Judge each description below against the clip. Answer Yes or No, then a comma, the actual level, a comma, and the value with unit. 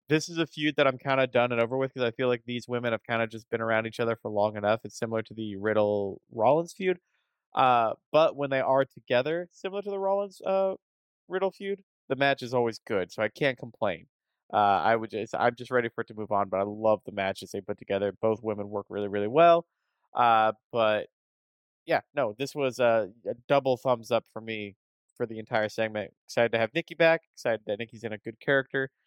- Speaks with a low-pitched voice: Yes, low, 120 Hz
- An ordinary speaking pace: No, fast, 235 wpm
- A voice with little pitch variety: No, average, 4.2 semitones